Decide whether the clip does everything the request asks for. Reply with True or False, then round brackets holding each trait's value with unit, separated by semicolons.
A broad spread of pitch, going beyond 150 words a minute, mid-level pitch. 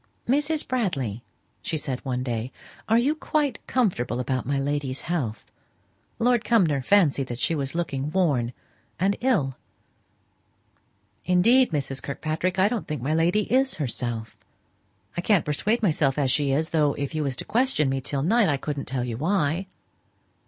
True (7.0 semitones; 160 wpm; 150 Hz)